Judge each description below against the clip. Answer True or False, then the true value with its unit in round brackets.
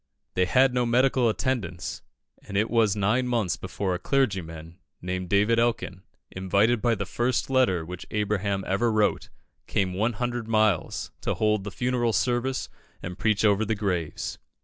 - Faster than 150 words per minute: True (160 wpm)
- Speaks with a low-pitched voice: True (105 Hz)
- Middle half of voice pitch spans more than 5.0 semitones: False (4.2 semitones)